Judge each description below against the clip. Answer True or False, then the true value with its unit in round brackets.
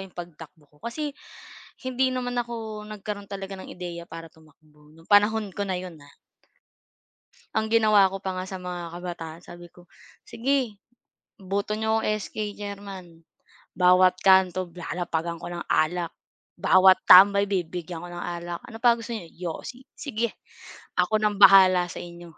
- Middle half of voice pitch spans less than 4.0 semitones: True (3.5 semitones)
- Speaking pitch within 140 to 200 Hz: True (185 Hz)